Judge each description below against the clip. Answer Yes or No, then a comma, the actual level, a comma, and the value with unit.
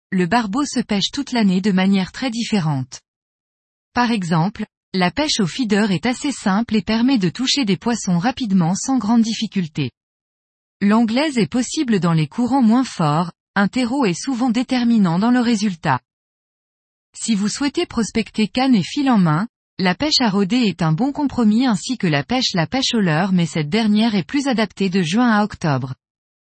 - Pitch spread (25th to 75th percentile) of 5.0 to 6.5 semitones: Yes, wide, 5.5 semitones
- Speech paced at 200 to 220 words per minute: No, average, 180 wpm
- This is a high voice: Yes, high, 215 Hz